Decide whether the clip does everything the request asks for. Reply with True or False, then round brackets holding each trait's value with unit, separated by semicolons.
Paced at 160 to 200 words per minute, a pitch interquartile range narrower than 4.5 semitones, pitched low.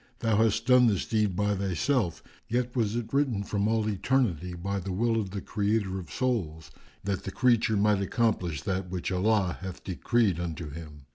True (185 wpm; 3.7 semitones; 100 Hz)